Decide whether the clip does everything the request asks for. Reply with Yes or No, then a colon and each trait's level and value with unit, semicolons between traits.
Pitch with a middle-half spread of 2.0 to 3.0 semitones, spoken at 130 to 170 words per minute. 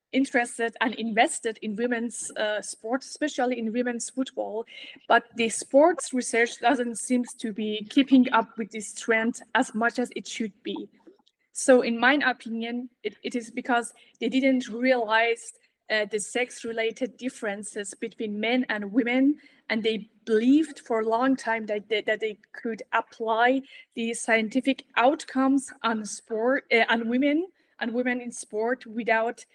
Yes: narrow, 2.4 semitones; average, 155 wpm